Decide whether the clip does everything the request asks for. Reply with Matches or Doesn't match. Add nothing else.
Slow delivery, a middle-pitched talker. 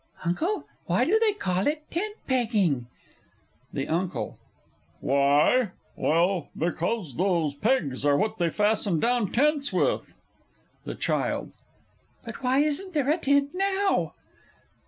Doesn't match